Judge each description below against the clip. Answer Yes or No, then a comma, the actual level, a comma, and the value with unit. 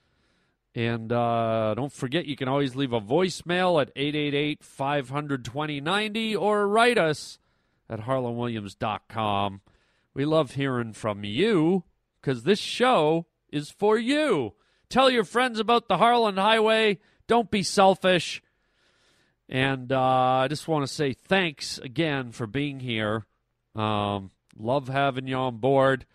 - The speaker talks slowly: Yes, slow, 130 wpm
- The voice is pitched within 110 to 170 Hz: Yes, medium, 140 Hz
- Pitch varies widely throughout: Yes, wide, 7.8 semitones